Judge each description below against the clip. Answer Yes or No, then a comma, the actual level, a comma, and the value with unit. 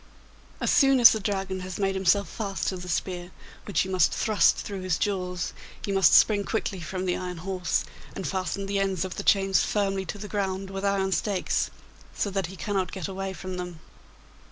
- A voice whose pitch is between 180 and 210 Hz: Yes, high, 190 Hz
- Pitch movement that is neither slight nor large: No, narrow, 1.4 semitones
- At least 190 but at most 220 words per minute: Yes, fast, 205 wpm